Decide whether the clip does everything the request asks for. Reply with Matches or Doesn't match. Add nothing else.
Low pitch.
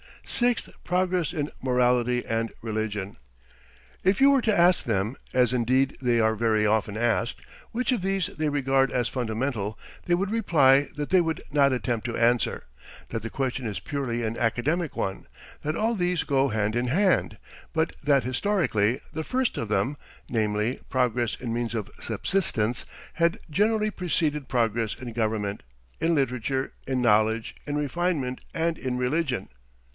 Matches